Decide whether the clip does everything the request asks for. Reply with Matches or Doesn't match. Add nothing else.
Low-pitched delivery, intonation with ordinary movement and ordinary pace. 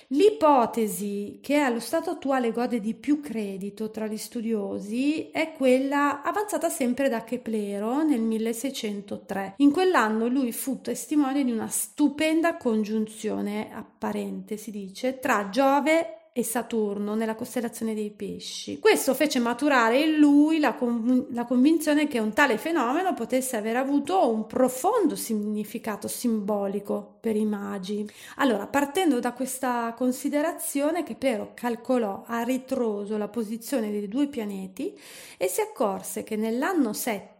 Doesn't match